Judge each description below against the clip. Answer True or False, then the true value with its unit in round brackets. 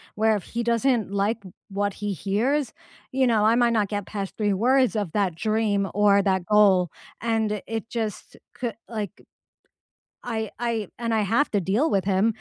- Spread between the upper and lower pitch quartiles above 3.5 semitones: False (2.5 semitones)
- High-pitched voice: True (215 Hz)